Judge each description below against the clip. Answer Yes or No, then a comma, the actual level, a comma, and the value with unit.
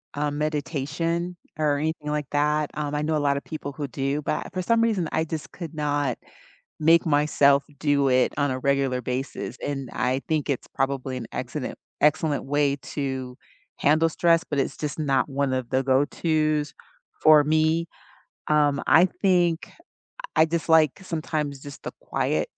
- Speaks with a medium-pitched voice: Yes, medium, 150 Hz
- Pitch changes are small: Yes, narrow, 2.2 semitones